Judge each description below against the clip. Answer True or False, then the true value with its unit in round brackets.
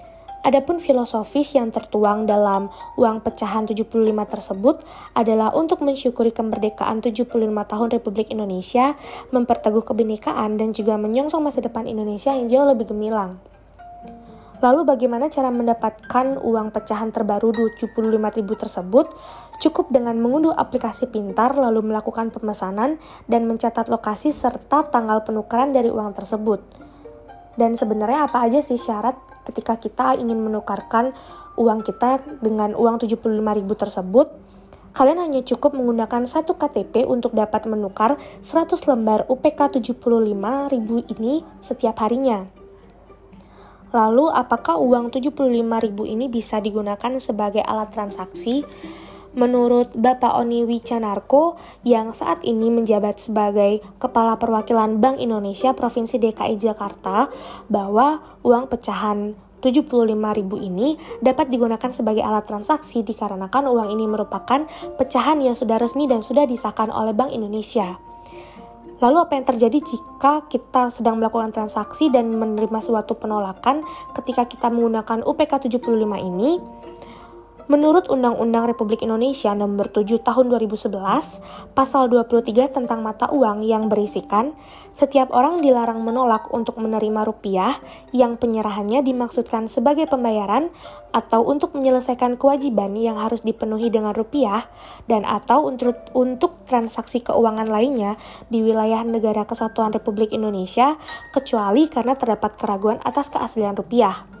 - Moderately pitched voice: False (230 Hz)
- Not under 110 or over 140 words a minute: True (125 wpm)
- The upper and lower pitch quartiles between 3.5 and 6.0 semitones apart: False (3.1 semitones)